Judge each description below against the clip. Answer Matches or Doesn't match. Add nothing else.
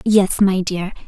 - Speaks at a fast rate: Doesn't match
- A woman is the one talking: Matches